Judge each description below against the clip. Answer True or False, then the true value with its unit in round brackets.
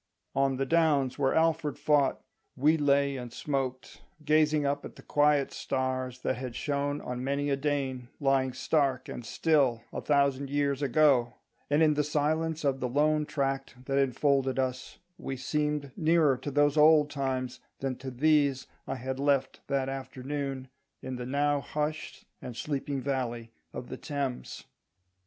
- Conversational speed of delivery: True (160 wpm)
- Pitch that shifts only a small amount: True (2.1 semitones)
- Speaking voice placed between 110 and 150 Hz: True (140 Hz)